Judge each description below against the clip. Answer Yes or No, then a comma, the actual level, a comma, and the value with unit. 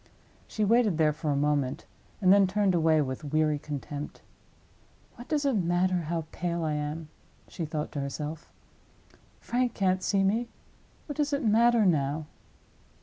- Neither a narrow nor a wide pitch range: No, wide, 5.7 semitones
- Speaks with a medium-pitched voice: Yes, medium, 170 Hz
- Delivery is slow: No, average, 150 wpm